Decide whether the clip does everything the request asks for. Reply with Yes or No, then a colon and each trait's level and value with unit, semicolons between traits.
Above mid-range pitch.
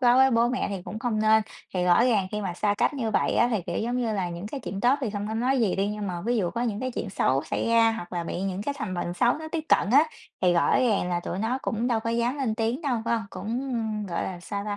Yes: high, 220 Hz